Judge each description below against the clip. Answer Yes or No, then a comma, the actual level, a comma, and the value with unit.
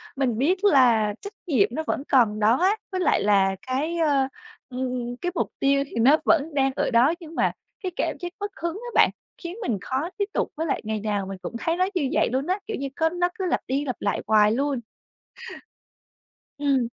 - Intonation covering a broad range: Yes, wide, 6.3 semitones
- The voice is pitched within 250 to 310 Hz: Yes, very high, 275 Hz